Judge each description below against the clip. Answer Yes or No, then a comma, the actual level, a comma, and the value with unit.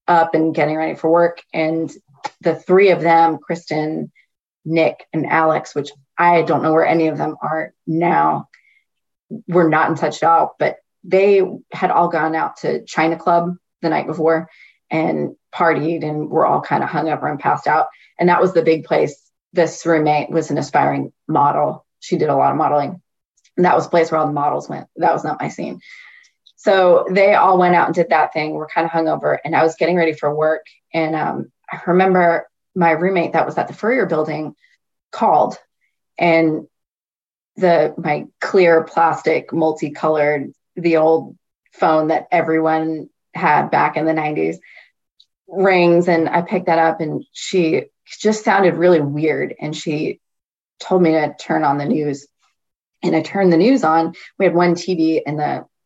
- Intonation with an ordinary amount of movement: No, narrow, 1.8 semitones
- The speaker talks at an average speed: Yes, average, 180 wpm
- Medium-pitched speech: Yes, medium, 165 Hz